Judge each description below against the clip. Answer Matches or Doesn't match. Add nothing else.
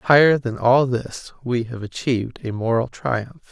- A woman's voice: Doesn't match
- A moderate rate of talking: Matches